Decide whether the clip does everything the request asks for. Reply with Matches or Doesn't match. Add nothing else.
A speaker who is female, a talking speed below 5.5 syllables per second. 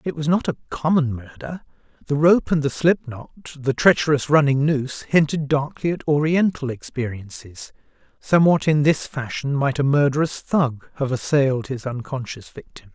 Doesn't match